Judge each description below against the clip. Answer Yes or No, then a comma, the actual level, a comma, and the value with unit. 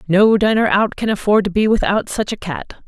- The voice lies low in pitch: No, high, 200 Hz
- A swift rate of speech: Yes, fast, 230 wpm